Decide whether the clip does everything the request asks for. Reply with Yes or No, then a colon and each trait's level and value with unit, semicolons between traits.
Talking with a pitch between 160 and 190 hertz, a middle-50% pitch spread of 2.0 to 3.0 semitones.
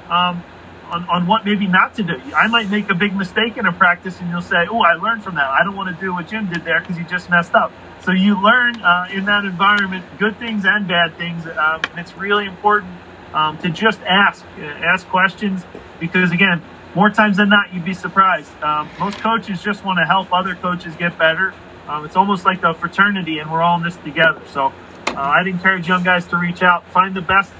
Yes: medium, 185 Hz; average, 2.7 semitones